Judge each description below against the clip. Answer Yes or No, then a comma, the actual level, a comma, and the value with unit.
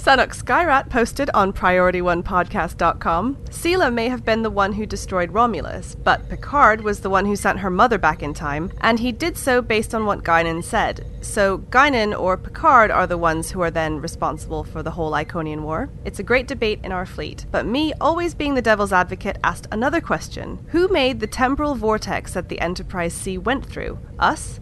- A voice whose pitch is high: Yes, high, 210 Hz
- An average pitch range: No, wide, 5.7 semitones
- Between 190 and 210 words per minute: Yes, average, 195 wpm